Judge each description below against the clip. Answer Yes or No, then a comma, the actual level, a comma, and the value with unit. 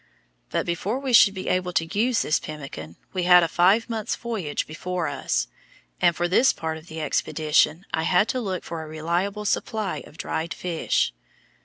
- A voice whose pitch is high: No, medium, 175 Hz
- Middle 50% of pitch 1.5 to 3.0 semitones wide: No, average, 4.1 semitones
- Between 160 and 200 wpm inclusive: Yes, average, 185 wpm